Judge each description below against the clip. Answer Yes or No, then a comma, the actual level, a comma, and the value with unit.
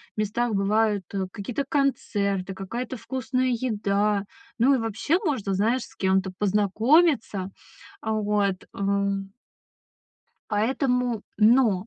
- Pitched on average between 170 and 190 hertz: No, high, 210 Hz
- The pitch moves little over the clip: No, average, 3.8 semitones